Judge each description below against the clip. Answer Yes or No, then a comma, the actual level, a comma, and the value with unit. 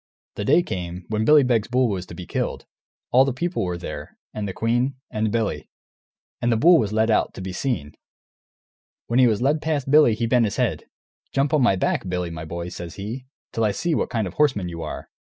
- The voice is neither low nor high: No, low, 110 Hz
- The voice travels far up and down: Yes, wide, 5.9 semitones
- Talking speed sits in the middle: No, fast, 230 wpm